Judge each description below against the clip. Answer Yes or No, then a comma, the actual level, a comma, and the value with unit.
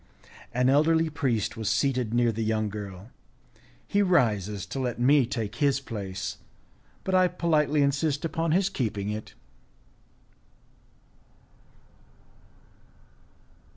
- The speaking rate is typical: No, slow, 110 wpm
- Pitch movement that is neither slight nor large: No, wide, 6.0 semitones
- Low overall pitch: Yes, low, 125 Hz